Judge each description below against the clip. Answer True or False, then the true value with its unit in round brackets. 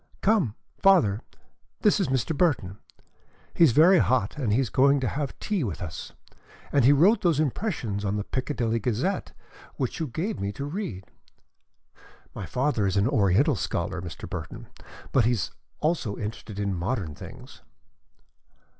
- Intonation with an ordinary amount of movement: False (7.3 semitones)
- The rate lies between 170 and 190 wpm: False (160 wpm)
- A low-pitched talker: True (125 Hz)